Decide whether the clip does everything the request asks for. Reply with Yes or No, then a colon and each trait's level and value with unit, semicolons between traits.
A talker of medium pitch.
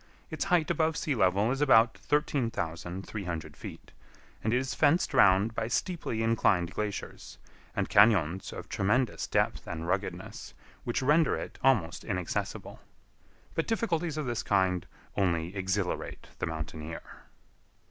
No: low, 110 Hz